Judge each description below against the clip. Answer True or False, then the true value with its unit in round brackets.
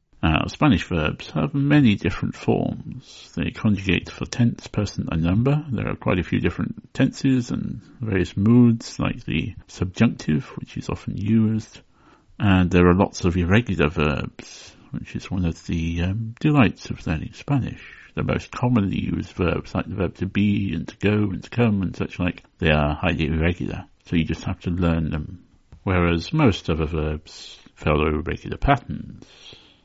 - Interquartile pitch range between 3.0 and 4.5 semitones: False (5.0 semitones)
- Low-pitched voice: True (90 Hz)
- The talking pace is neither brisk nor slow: True (170 wpm)